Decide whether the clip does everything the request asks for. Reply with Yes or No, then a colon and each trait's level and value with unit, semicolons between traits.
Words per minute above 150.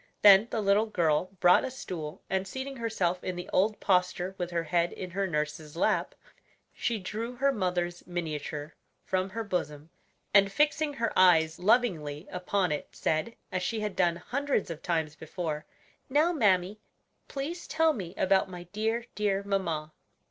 Yes: average, 160 wpm